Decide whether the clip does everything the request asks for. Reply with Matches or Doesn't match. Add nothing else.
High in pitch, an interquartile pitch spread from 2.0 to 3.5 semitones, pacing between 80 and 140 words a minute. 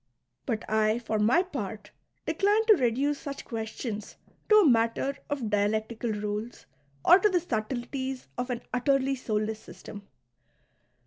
Doesn't match